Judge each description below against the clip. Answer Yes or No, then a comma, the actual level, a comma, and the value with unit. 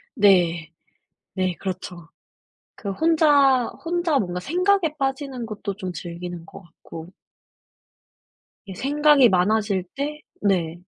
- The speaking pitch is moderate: No, high, 205 Hz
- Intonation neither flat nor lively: No, wide, 8.1 semitones